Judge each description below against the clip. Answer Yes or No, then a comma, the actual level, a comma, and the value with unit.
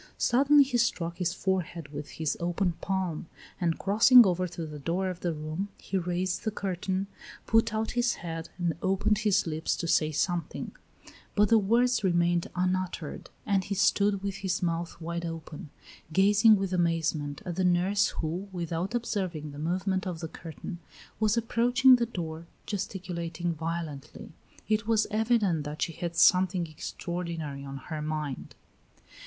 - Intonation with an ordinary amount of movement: Yes, average, 3.3 semitones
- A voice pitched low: No, medium, 180 Hz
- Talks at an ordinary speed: Yes, average, 160 wpm